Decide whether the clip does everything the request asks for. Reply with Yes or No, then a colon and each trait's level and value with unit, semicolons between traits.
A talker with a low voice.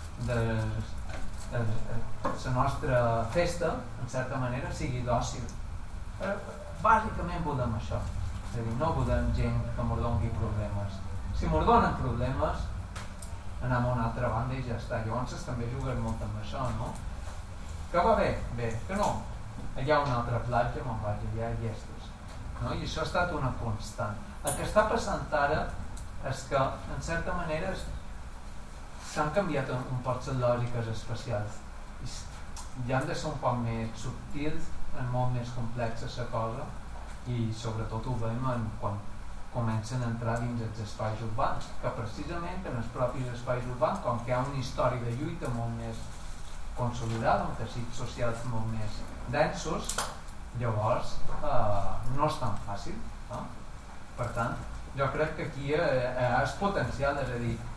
Yes: low, 115 Hz